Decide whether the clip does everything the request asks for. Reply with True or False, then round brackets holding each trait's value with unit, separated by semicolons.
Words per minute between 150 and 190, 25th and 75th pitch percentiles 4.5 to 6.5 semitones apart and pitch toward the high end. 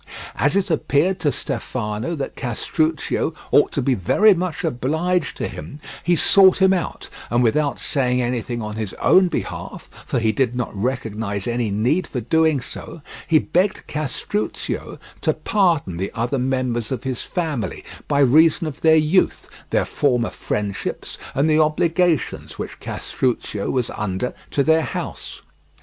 False (155 wpm; 5.2 semitones; 140 Hz)